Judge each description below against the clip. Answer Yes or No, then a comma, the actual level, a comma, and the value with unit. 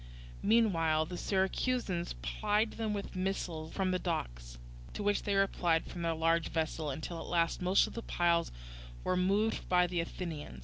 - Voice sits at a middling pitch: Yes, medium, 175 Hz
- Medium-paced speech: Yes, average, 170 wpm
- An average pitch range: Yes, average, 3.2 semitones